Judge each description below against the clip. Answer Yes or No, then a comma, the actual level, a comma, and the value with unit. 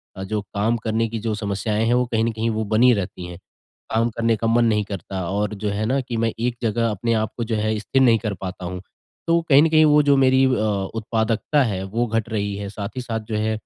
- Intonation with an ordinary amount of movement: No, narrow, 2.2 semitones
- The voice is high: No, low, 110 Hz